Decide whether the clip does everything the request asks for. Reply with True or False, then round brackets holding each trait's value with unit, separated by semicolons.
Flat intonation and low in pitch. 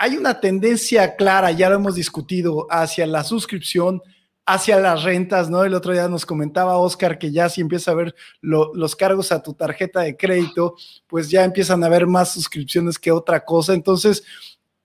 False (2.1 semitones; 180 Hz)